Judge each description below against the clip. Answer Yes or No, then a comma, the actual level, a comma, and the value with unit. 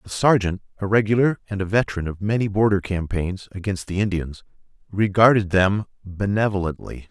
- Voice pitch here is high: No, low, 100 Hz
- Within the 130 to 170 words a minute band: Yes, average, 145 wpm